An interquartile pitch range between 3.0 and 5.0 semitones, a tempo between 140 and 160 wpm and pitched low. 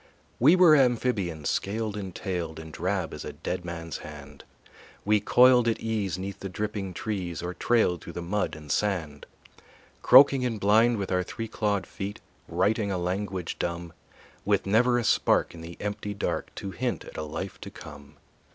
No: average, 4.2 semitones; average, 180 wpm; low, 100 Hz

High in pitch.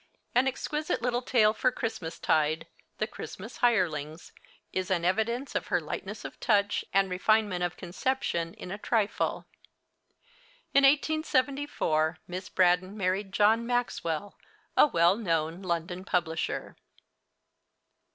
Yes: high, 195 Hz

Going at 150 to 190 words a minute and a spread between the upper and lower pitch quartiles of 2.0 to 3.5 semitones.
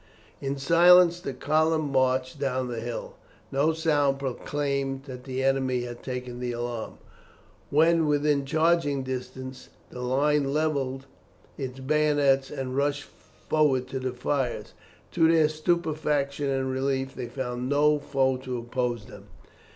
No: slow, 135 wpm; narrow, 2.5 semitones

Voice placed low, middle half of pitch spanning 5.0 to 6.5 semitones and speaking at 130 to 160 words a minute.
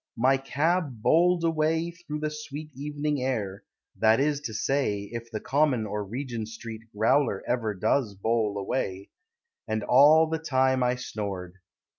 Yes: low, 130 Hz; wide, 5.4 semitones; average, 150 wpm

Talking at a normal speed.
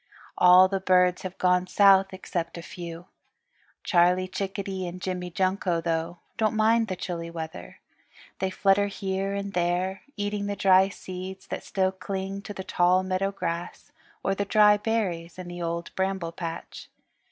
Yes: average, 160 wpm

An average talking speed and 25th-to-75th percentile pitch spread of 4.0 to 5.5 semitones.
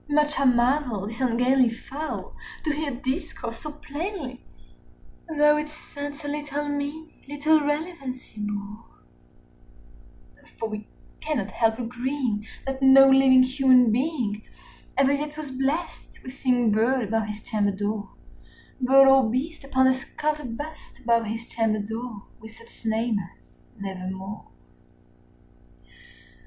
No: slow, 130 wpm; average, 4.5 semitones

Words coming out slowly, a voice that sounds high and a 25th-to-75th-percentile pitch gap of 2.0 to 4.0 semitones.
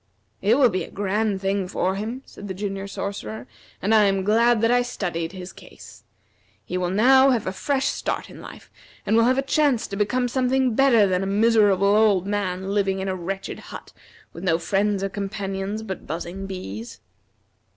No: average, 195 wpm; high, 200 Hz; average, 3.2 semitones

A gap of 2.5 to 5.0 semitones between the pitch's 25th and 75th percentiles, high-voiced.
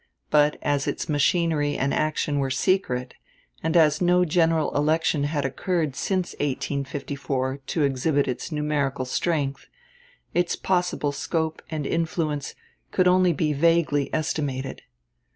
No: average, 2.9 semitones; medium, 150 Hz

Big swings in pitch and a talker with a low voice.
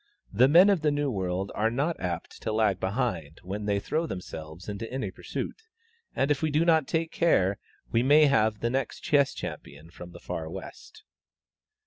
Yes: wide, 7.7 semitones; low, 115 Hz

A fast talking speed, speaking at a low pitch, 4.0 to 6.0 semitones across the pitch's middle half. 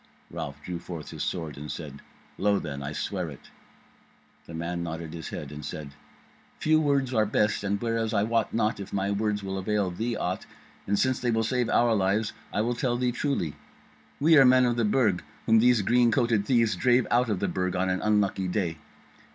Yes: fast, 210 wpm; low, 105 Hz; average, 5.0 semitones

